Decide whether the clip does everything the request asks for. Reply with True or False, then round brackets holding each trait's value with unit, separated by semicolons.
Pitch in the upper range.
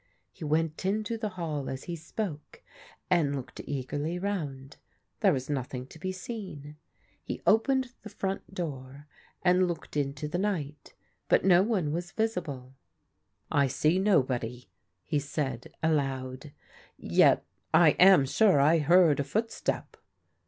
False (155 Hz)